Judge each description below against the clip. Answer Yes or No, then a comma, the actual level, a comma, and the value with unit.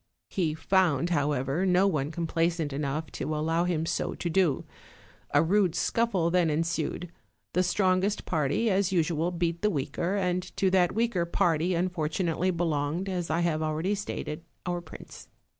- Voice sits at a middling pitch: Yes, medium, 170 Hz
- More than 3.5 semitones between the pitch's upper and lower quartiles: No, average, 2.8 semitones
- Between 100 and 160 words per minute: Yes, average, 155 wpm